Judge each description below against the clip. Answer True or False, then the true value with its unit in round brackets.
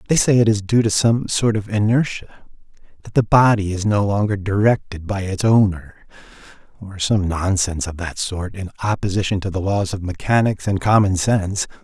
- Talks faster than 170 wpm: True (185 wpm)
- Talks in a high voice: False (100 Hz)